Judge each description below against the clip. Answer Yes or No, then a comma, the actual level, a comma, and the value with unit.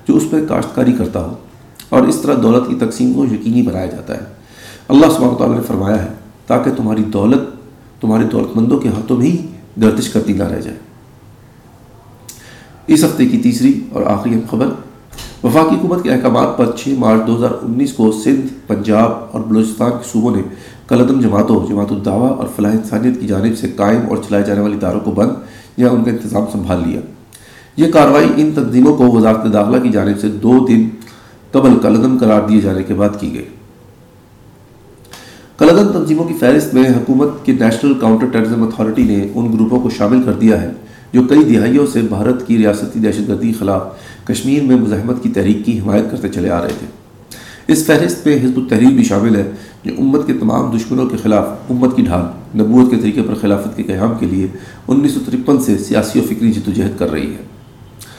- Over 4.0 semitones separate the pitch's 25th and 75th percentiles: No, average, 3.2 semitones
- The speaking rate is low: No, fast, 190 wpm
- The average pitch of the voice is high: No, low, 115 Hz